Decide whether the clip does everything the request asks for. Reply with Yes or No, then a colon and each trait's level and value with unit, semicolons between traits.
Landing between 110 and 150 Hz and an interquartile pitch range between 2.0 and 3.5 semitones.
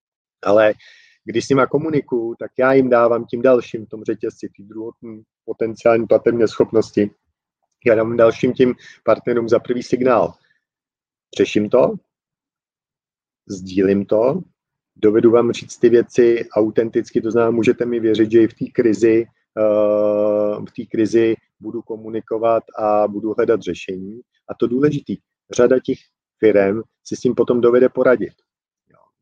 Yes: low, 115 Hz; narrow, 2.4 semitones